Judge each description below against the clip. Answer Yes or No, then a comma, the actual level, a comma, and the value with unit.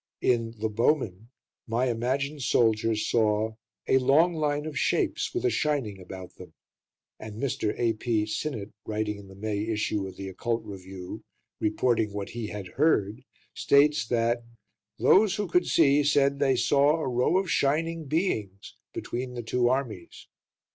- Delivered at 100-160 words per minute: Yes, average, 155 wpm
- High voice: No, low, 120 Hz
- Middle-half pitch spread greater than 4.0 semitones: Yes, average, 5.1 semitones